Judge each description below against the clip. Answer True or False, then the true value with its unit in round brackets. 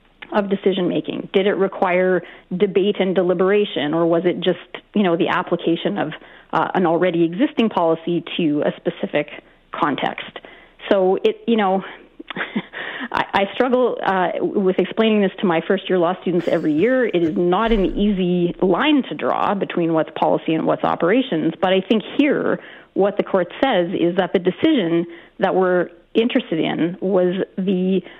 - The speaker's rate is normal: True (165 wpm)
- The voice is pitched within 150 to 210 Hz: True (185 Hz)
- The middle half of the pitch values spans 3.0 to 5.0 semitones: False (2.6 semitones)